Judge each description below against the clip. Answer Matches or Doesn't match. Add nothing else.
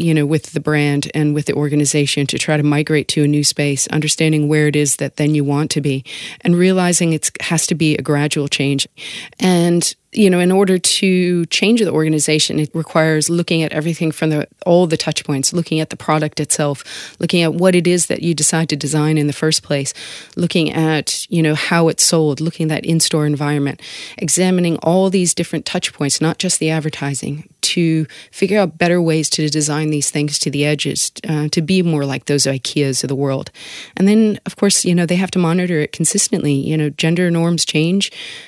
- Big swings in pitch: Doesn't match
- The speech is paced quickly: Matches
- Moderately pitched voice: Matches